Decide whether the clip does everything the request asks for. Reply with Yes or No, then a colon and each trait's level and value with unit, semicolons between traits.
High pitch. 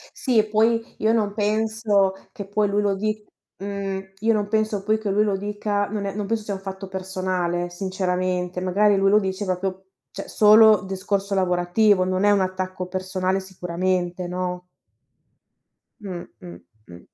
Yes: high, 195 Hz